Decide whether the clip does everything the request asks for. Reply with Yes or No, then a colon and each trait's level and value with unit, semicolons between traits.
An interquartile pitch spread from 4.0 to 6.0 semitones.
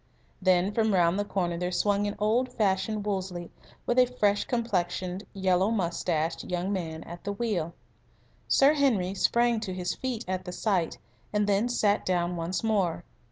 No: average, 3.4 semitones